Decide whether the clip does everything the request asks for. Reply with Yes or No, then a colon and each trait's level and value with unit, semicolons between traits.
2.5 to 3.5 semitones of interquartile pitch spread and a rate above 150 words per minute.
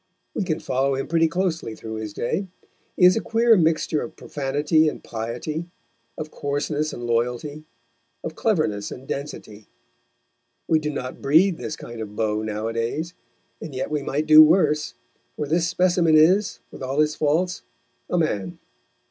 No: average, 4.9 semitones; average, 160 wpm